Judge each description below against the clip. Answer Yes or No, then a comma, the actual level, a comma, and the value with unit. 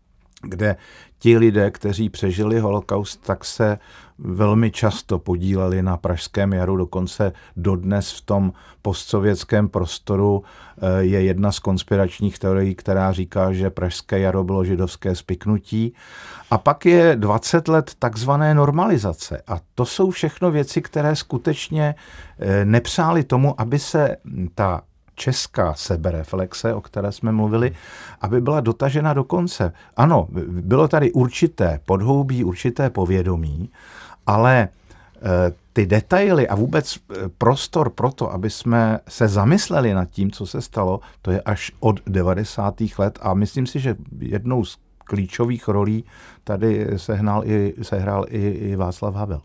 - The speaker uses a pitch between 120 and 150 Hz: No, low, 105 Hz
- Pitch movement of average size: Yes, average, 4.0 semitones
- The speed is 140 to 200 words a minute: No, average, 130 wpm